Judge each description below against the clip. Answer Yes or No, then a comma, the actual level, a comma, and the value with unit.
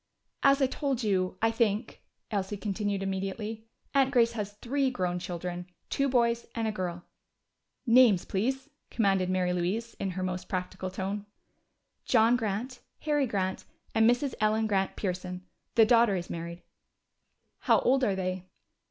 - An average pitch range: Yes, average, 4.1 semitones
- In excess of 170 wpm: No, average, 150 wpm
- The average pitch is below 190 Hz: No, high, 210 Hz